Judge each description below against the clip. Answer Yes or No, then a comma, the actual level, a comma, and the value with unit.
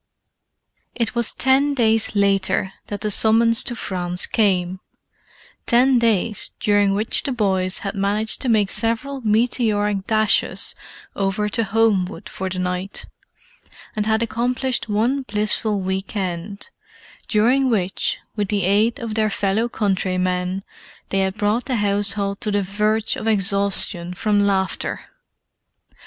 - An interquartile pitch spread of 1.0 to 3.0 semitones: Yes, narrow, 2.6 semitones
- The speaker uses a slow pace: Yes, slow, 130 wpm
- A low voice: No, high, 210 Hz